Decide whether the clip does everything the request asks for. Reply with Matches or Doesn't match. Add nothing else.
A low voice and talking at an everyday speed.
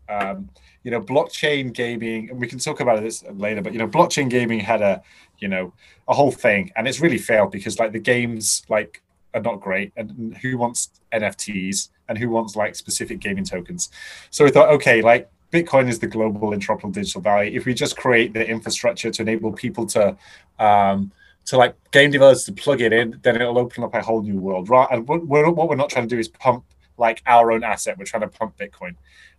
Doesn't match